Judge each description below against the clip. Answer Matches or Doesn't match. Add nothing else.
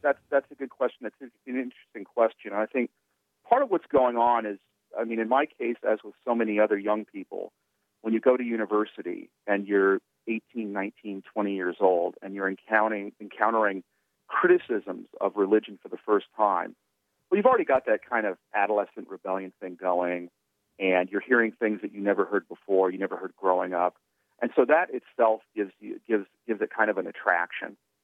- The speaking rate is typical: Matches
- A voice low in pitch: Matches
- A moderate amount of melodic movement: Matches